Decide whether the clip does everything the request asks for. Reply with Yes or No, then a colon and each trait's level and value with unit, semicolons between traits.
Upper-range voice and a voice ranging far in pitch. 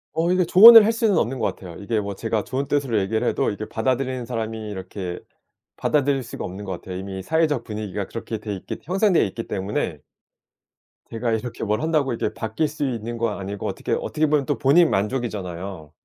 No: low, 115 Hz; wide, 5.8 semitones